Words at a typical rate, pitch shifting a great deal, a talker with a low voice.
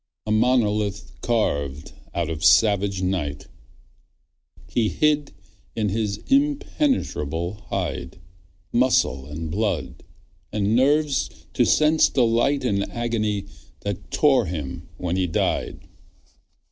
No: slow, 105 wpm; wide, 6.2 semitones; low, 105 Hz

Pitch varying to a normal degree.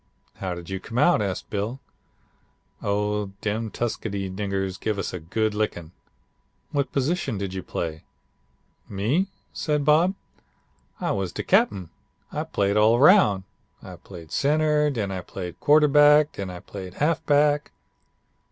No: wide, 7.2 semitones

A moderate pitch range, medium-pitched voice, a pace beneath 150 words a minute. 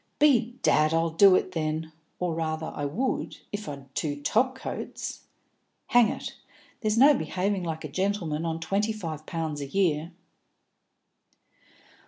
Yes: average, 5.0 semitones; medium, 165 Hz; average, 140 wpm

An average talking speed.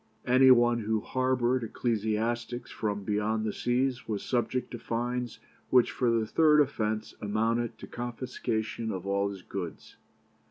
Yes: average, 145 wpm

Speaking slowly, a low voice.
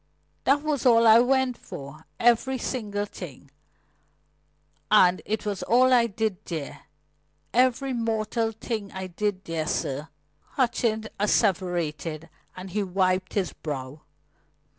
No: slow, 120 wpm; high, 210 Hz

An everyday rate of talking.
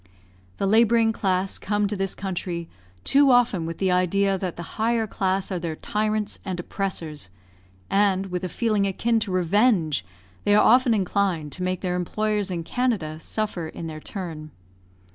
Yes: average, 165 wpm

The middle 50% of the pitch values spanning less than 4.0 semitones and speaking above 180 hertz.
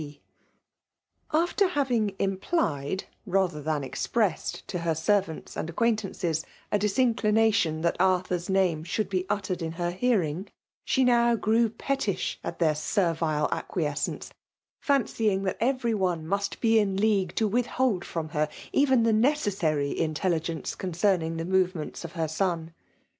No: average, 5.2 semitones; high, 190 Hz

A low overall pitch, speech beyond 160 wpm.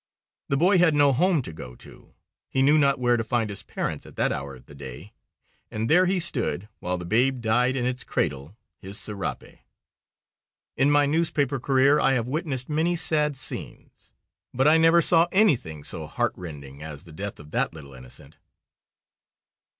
Yes: low, 125 Hz; average, 180 wpm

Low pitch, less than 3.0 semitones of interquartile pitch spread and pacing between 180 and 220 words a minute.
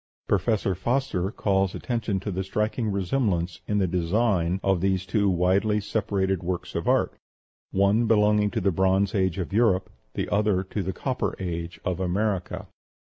No: very low, 95 Hz; narrow, 2.4 semitones; average, 160 wpm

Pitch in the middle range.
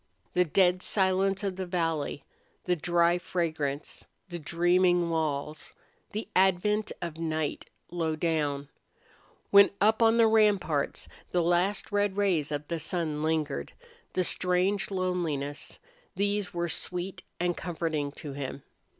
Yes: medium, 175 Hz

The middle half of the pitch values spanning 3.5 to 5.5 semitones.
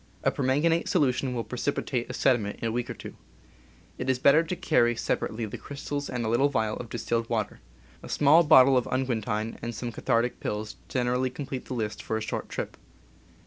No: average, 3.1 semitones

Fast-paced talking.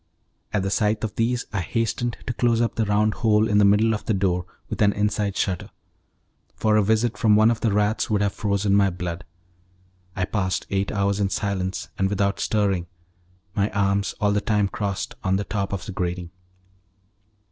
No: average, 195 wpm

